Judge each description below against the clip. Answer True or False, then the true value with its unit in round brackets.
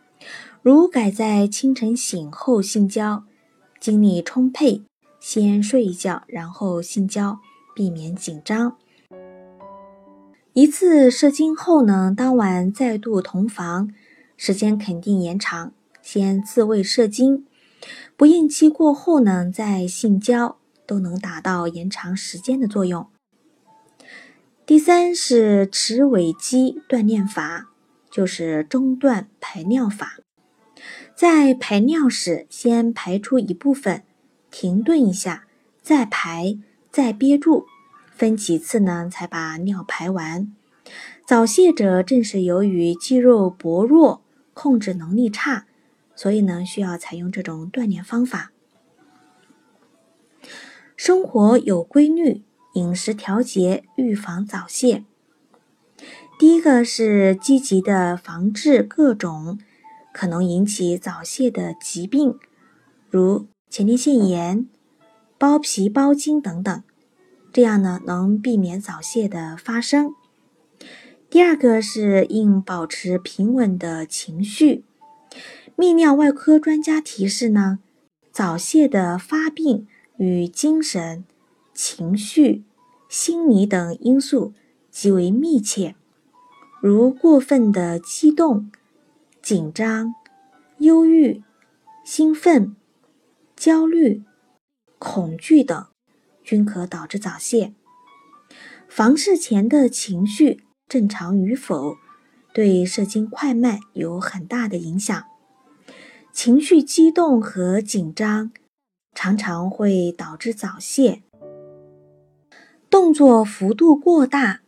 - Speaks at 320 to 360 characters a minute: False (155 characters per minute)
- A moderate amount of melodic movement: False (6.4 semitones)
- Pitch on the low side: False (220 Hz)